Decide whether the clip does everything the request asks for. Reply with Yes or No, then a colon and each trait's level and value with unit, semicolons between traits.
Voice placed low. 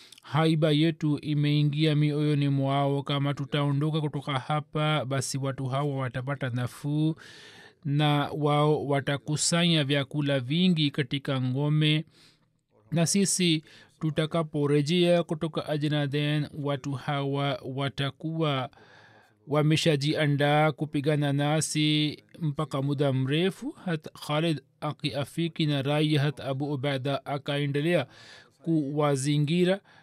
No: medium, 150 Hz